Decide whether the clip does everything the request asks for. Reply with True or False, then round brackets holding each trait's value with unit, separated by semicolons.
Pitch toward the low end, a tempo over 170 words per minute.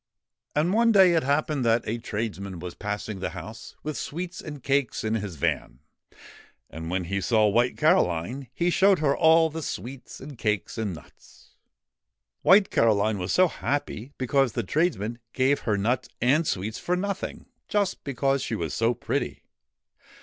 False (125 Hz; 165 wpm)